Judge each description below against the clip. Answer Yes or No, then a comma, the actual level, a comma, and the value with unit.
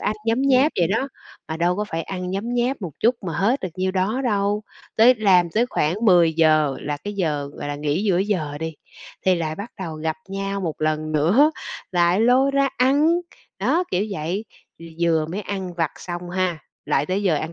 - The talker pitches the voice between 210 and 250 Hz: No, medium, 185 Hz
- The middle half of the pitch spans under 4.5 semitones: No, average, 4.8 semitones